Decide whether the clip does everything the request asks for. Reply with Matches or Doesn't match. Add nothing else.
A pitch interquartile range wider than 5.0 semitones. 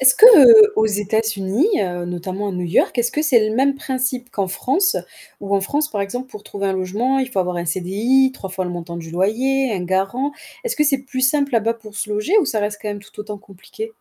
Matches